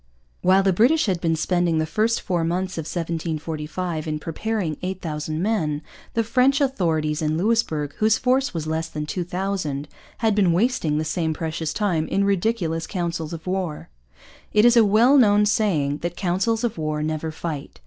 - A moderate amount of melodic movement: Yes, average, 4.9 semitones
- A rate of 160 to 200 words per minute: Yes, average, 170 wpm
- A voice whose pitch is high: No, medium, 175 Hz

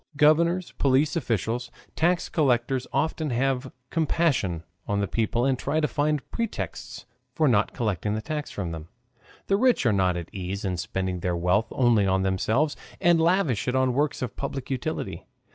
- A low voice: Yes, low, 125 Hz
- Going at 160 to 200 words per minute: Yes, average, 170 wpm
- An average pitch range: No, wide, 7.2 semitones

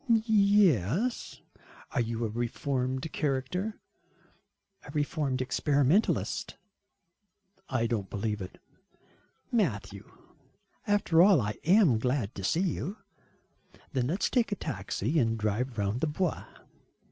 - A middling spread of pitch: No, wide, 8.1 semitones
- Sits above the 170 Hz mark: No, low, 135 Hz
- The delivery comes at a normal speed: No, slow, 115 wpm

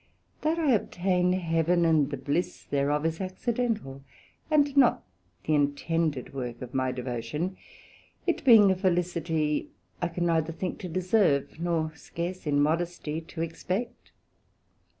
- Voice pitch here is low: No, medium, 165 Hz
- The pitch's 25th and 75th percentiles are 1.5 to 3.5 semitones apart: No, average, 3.9 semitones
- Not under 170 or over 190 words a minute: No, slow, 135 wpm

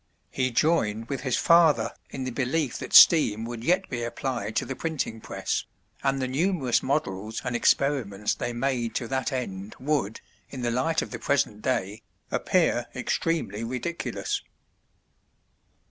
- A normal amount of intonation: Yes, average, 3.9 semitones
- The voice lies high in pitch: No, low, 130 Hz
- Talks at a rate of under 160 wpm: Yes, average, 150 wpm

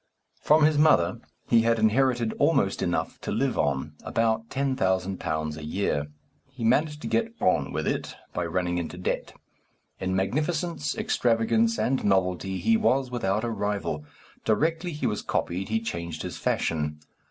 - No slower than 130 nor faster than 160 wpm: Yes, average, 155 wpm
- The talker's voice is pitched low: Yes, low, 110 Hz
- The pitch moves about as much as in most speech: No, wide, 7.1 semitones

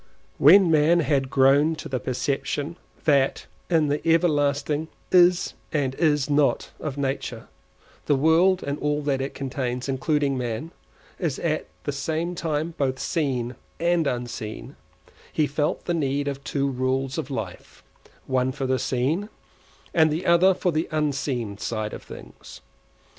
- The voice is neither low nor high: Yes, medium, 145 Hz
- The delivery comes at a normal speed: Yes, average, 145 wpm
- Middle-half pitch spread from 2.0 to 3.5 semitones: Yes, average, 3.2 semitones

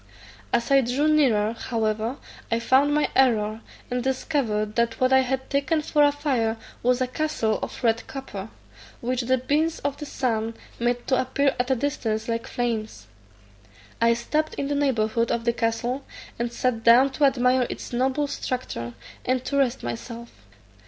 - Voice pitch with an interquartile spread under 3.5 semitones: Yes, average, 3.1 semitones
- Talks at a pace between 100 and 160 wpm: No, average, 170 wpm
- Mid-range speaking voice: No, very high, 250 Hz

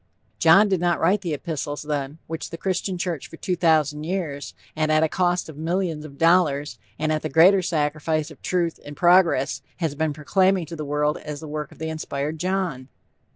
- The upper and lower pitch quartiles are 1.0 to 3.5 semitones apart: Yes, average, 2.9 semitones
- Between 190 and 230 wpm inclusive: Yes, average, 200 wpm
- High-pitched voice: No, medium, 160 Hz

